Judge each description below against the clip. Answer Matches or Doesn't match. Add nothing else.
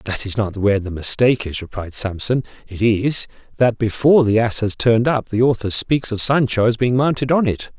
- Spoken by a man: Matches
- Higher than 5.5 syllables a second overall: Doesn't match